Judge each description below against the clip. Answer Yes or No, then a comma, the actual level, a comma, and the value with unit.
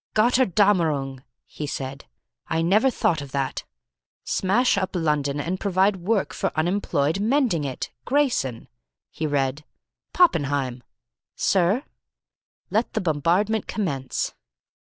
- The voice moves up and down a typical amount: No, wide, 6.5 semitones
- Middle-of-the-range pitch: Yes, medium, 170 Hz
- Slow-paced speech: Yes, slow, 110 wpm